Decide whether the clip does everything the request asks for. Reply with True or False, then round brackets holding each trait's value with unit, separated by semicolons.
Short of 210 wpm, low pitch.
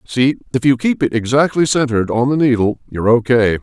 True (200 wpm; 125 Hz)